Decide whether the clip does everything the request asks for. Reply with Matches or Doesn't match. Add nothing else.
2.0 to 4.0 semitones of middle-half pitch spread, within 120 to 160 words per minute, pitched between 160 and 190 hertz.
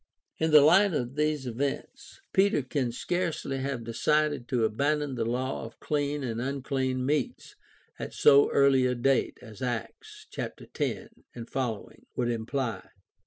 Doesn't match